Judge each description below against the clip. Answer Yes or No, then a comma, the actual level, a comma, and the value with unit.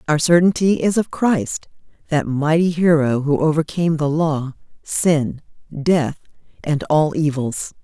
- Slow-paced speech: Yes, slow, 130 wpm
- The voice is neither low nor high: Yes, medium, 155 Hz